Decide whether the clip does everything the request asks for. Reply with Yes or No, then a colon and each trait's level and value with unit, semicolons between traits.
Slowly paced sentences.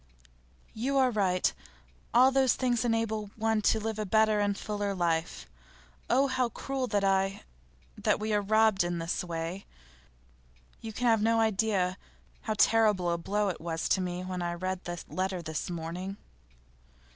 No: average, 165 wpm